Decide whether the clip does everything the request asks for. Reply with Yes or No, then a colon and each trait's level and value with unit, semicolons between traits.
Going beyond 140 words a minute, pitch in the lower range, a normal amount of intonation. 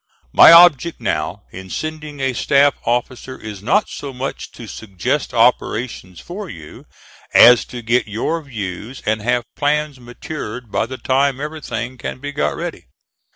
Yes: average, 155 wpm; low, 125 Hz; average, 4.6 semitones